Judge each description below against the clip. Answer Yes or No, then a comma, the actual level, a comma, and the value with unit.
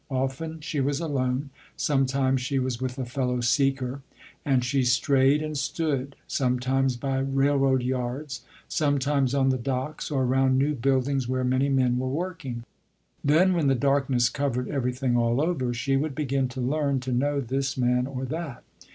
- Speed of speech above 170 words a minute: No, average, 165 wpm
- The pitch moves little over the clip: Yes, narrow, 1.8 semitones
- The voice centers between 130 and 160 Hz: Yes, low, 135 Hz